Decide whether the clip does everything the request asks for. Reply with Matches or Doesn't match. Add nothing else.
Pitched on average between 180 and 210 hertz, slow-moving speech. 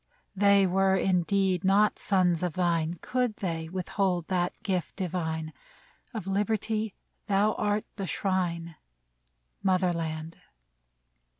Matches